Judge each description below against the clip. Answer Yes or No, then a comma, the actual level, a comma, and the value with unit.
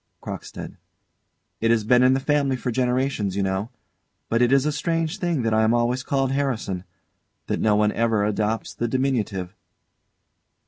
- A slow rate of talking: No, average, 175 wpm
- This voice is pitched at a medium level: No, low, 120 Hz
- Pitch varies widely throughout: No, average, 3.8 semitones